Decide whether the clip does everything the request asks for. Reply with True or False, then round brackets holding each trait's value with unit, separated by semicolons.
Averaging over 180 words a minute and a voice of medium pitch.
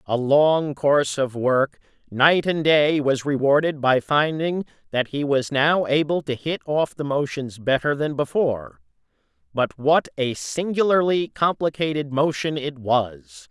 False (145 wpm; 145 Hz)